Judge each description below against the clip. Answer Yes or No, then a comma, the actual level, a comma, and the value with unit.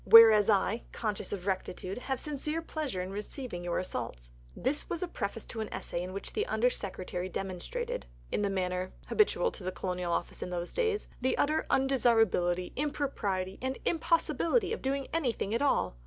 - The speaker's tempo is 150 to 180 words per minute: Yes, average, 175 wpm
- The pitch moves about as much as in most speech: No, wide, 7.6 semitones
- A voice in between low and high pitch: No, high, 225 Hz